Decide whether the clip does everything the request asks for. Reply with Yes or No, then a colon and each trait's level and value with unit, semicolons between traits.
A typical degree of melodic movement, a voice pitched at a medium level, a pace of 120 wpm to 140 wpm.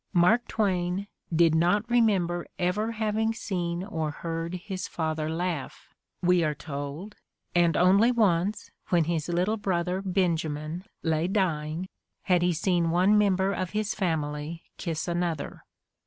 Yes: average, 3.1 semitones; medium, 175 Hz; slow, 135 wpm